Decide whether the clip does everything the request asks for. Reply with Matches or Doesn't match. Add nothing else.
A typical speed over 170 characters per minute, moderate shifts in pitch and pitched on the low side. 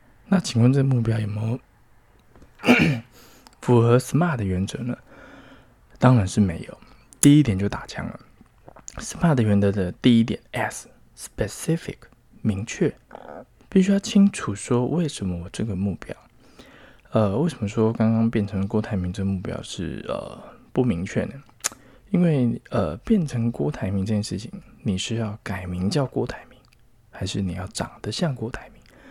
Matches